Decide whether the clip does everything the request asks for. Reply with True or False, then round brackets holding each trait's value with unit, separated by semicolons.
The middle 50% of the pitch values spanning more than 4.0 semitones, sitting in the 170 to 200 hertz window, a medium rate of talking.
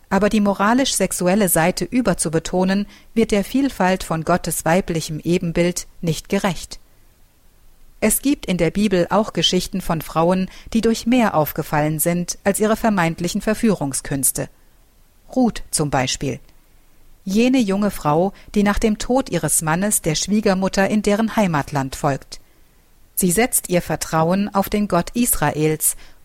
True (4.7 semitones; 185 Hz; 135 wpm)